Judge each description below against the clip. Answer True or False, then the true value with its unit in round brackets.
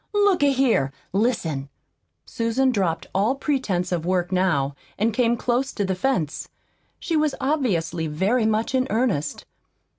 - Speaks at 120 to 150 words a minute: True (145 wpm)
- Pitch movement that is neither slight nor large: False (6.7 semitones)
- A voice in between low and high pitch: False (220 Hz)